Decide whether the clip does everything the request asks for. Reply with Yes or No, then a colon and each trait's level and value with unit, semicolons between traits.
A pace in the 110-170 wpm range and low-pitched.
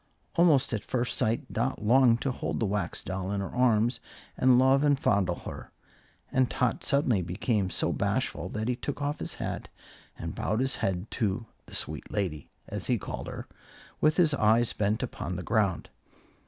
No: average, 180 wpm; low, 115 Hz